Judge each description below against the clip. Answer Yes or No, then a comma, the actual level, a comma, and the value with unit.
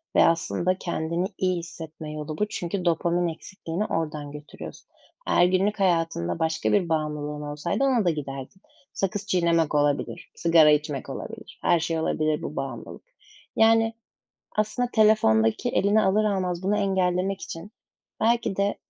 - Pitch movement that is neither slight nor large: Yes, average, 4.2 semitones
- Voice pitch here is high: No, medium, 170 Hz